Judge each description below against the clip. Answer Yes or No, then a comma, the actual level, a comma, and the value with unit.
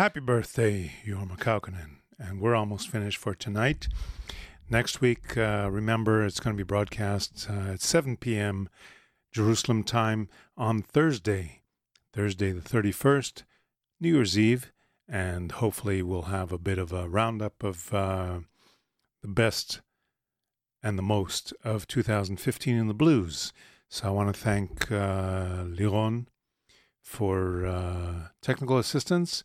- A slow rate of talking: Yes, slow, 130 wpm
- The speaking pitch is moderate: No, low, 105 Hz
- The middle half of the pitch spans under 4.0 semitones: Yes, average, 3.3 semitones